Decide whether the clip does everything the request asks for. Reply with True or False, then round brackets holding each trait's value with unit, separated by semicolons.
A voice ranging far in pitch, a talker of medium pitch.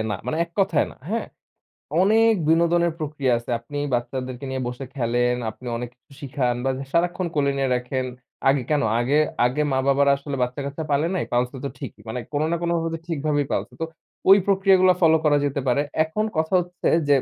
False (4.5 semitones; 145 Hz)